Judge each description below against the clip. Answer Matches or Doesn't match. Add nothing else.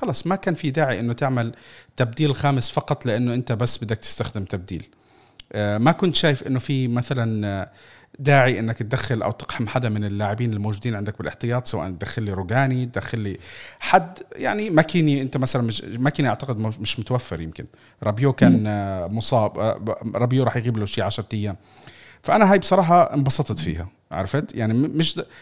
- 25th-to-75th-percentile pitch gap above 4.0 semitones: Matches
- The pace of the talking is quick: Matches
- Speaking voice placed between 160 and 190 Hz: Doesn't match